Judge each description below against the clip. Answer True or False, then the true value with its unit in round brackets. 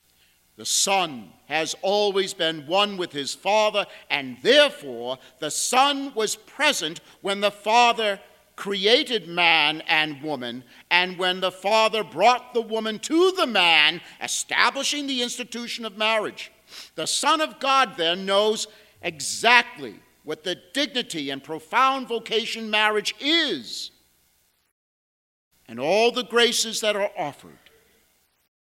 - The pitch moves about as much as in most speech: False (7.3 semitones)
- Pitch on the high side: True (200 Hz)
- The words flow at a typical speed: False (125 wpm)